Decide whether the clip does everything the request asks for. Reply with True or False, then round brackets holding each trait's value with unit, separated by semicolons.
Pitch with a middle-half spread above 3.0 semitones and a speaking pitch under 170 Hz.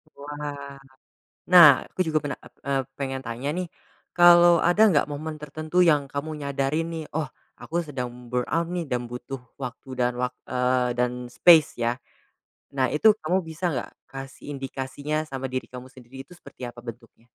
True (4.0 semitones; 140 Hz)